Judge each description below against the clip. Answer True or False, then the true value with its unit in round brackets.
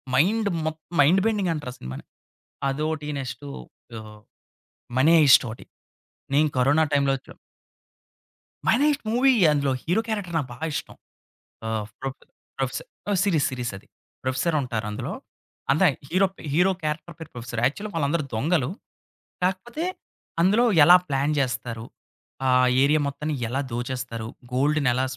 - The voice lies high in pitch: False (145 Hz)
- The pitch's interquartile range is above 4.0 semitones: True (5.1 semitones)